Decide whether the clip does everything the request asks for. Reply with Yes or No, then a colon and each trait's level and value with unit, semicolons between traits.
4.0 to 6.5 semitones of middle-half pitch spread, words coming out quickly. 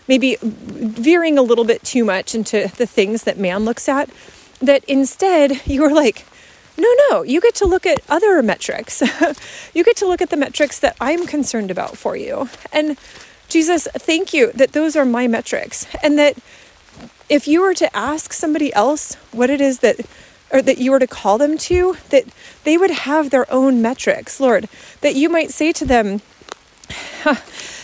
No: average, 4.6 semitones; average, 185 wpm